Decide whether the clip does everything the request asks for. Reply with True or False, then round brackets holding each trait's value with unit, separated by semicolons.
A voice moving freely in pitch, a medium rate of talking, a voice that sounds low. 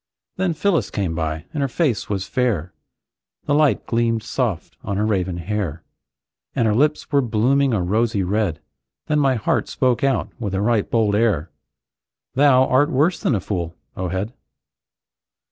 True (5.8 semitones; 165 wpm; 110 Hz)